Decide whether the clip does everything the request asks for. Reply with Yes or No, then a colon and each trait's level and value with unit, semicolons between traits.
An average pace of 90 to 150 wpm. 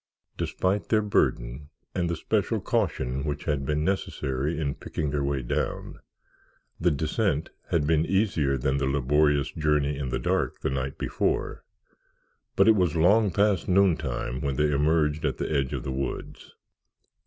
No: average, 160 wpm